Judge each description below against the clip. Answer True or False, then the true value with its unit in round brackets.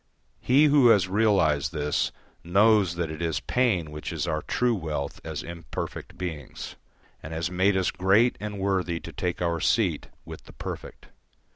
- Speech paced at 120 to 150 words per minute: False (165 wpm)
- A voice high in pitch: False (90 Hz)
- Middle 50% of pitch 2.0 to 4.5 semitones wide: True (4.2 semitones)